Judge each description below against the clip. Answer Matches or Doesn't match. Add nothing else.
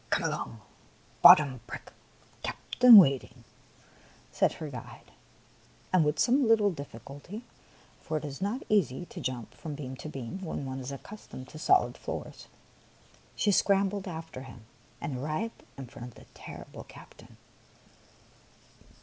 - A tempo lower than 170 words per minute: Matches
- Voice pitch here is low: Doesn't match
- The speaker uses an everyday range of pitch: Doesn't match